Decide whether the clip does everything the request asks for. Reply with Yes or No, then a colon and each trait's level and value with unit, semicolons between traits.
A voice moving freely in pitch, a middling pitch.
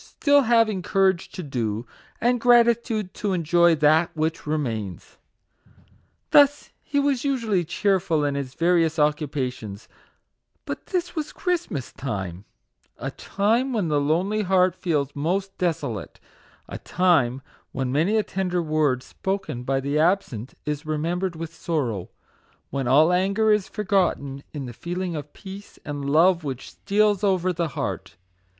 Yes: wide, 5.7 semitones; medium, 170 Hz